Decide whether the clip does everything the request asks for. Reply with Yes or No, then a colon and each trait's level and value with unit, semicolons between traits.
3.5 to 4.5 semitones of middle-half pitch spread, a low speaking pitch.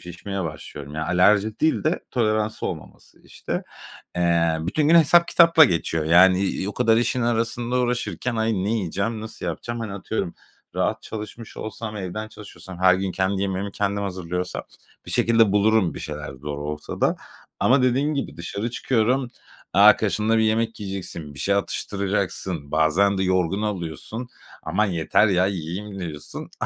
Yes: average, 4.2 semitones; low, 100 Hz